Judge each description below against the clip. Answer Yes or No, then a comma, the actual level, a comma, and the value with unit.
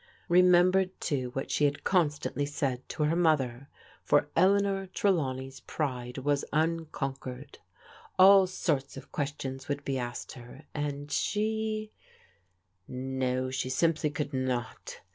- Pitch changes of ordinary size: Yes, average, 5.0 semitones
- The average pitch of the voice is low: No, medium, 145 Hz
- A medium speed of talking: No, slow, 125 wpm